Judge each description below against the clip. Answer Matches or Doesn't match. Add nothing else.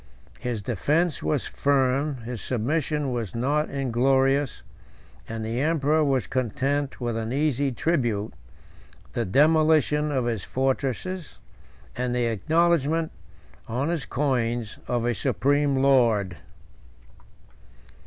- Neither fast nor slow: Doesn't match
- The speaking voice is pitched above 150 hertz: Doesn't match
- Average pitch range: Matches